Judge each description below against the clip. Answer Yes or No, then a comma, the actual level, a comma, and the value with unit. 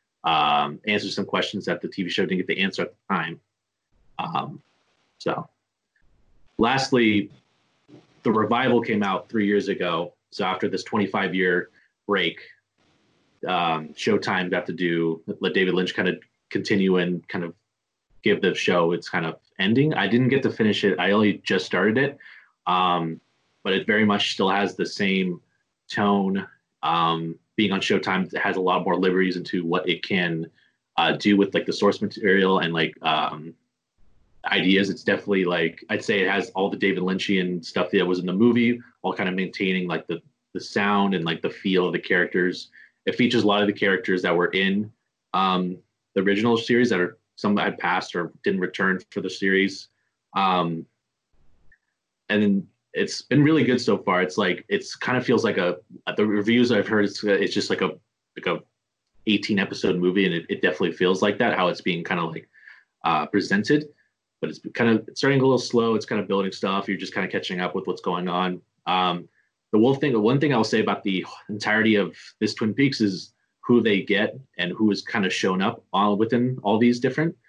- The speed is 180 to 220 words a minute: Yes, average, 200 wpm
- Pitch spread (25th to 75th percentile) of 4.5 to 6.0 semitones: No, average, 2.9 semitones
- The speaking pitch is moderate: No, low, 100 Hz